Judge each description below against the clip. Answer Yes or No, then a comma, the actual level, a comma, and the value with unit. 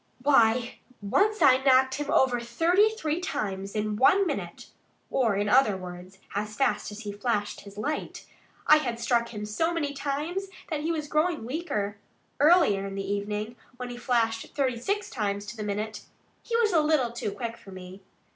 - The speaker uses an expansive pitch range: Yes, wide, 6.3 semitones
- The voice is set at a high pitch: Yes, high, 240 Hz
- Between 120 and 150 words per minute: No, average, 185 wpm